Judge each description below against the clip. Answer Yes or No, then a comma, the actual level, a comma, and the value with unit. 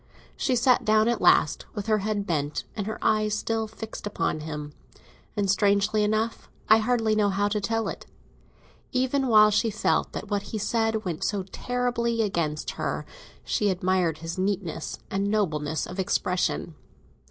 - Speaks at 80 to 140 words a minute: No, average, 155 wpm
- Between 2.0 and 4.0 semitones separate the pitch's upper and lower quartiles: Yes, average, 2.9 semitones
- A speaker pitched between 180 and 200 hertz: No, high, 210 Hz